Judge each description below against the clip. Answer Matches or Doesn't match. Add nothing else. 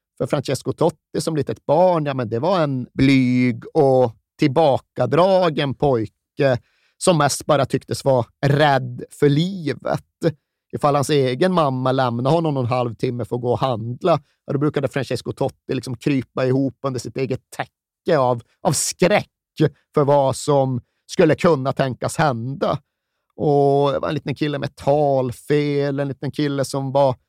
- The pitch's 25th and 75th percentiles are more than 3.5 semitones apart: Doesn't match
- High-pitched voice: Doesn't match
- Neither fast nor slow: Matches